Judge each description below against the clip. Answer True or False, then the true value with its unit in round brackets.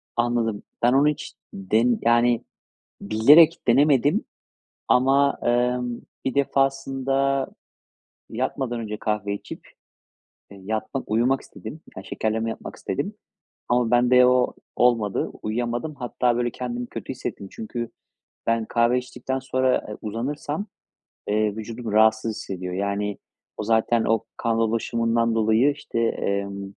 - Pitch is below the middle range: True (120 Hz)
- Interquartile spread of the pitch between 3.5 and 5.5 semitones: False (2.8 semitones)